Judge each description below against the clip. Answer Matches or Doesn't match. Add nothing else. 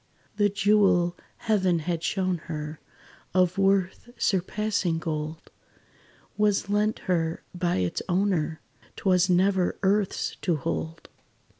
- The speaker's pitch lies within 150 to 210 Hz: Matches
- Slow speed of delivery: Matches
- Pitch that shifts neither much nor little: Matches